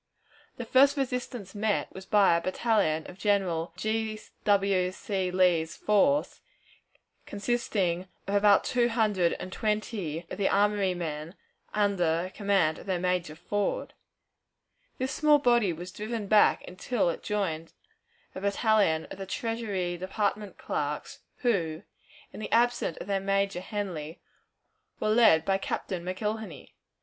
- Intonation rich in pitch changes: No, average, 3.3 semitones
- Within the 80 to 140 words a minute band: Yes, slow, 135 wpm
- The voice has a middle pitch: No, high, 200 Hz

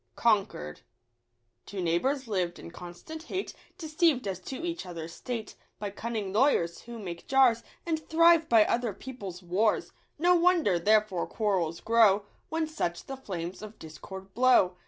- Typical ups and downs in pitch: No, wide, 6.7 semitones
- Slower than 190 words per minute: Yes, average, 150 wpm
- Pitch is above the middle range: Yes, high, 215 Hz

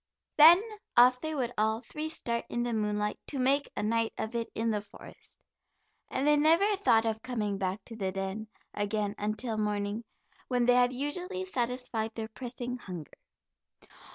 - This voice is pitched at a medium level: No, high, 235 Hz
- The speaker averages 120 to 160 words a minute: No, average, 170 wpm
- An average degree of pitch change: Yes, average, 3.4 semitones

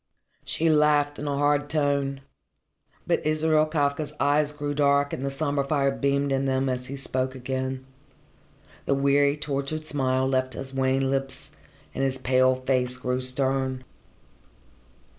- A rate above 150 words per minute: No, average, 145 wpm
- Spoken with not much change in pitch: Yes, narrow, 1.7 semitones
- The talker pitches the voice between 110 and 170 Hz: Yes, medium, 140 Hz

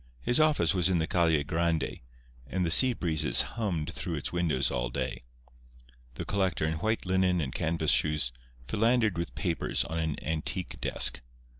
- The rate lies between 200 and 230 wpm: No, average, 165 wpm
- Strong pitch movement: No, average, 3.2 semitones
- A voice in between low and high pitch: No, very low, 85 Hz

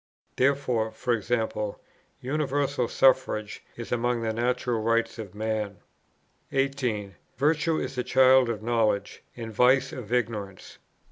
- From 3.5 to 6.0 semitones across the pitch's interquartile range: No, average, 3.1 semitones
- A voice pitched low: Yes, low, 120 Hz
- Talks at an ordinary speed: No, slow, 120 wpm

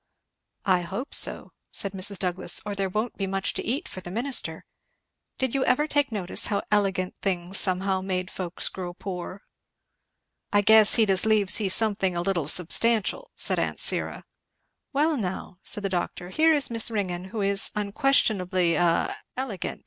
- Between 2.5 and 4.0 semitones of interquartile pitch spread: Yes, average, 3.3 semitones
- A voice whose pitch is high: Yes, high, 195 Hz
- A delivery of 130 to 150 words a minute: No, average, 170 wpm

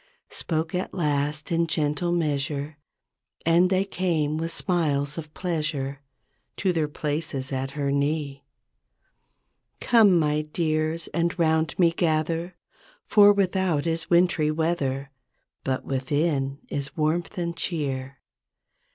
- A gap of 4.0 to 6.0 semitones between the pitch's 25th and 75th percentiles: No, average, 3.0 semitones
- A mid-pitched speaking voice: Yes, medium, 155 Hz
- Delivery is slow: Yes, slow, 115 wpm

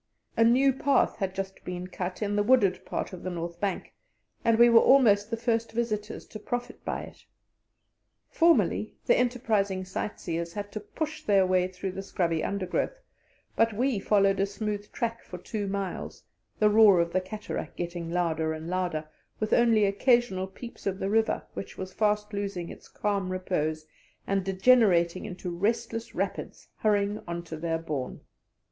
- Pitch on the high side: Yes, high, 200 Hz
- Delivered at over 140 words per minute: Yes, average, 170 wpm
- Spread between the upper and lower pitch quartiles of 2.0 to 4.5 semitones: Yes, average, 3.6 semitones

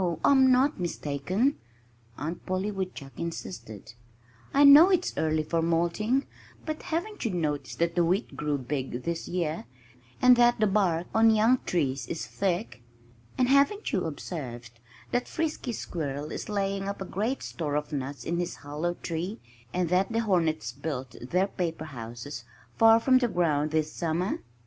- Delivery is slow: No, average, 160 wpm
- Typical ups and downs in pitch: No, wide, 6.8 semitones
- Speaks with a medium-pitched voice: Yes, medium, 175 Hz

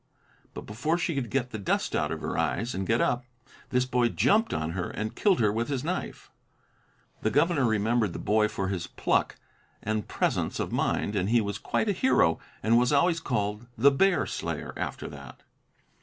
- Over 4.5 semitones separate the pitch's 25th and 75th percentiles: Yes, average, 5.1 semitones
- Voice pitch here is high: No, low, 115 Hz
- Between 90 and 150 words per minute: No, average, 195 wpm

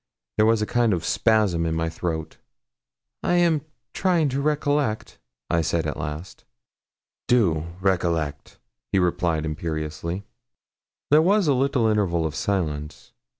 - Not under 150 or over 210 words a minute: No, slow, 135 wpm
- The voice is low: Yes, very low, 95 Hz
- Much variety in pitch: Yes, wide, 7.7 semitones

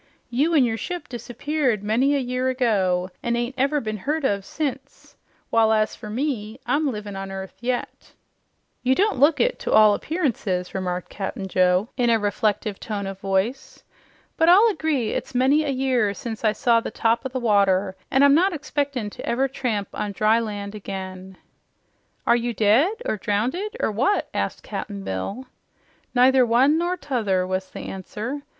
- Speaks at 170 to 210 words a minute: Yes, average, 175 wpm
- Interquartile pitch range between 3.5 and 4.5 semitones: No, average, 5.1 semitones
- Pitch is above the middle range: Yes, high, 235 Hz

